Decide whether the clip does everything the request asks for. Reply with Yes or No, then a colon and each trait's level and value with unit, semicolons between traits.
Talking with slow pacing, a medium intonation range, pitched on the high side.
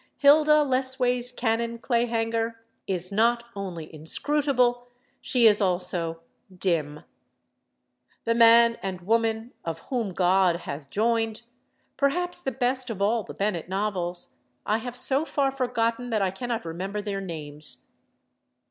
Yes: slow, 130 wpm; average, 4.9 semitones; high, 225 Hz